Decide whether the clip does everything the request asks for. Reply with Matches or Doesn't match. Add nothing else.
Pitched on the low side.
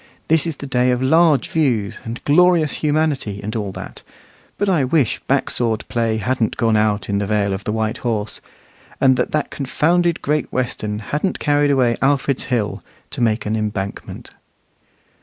Matches